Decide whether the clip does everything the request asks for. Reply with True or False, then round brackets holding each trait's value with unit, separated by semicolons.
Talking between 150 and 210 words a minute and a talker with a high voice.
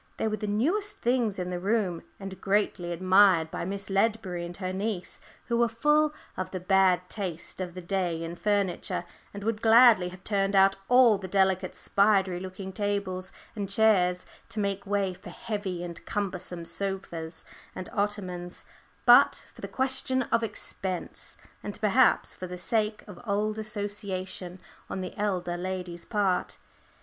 True (160 wpm; 195 Hz)